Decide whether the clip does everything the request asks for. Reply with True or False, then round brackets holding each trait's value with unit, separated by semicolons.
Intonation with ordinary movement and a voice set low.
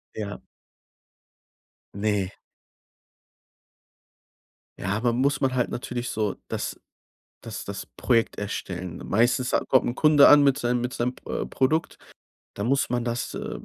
True (4.0 semitones; 120 Hz)